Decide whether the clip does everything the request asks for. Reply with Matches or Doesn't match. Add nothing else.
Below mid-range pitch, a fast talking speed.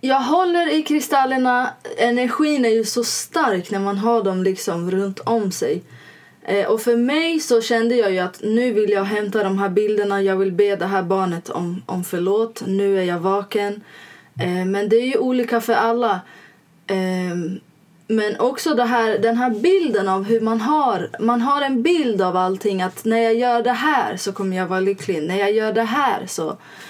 Doesn't match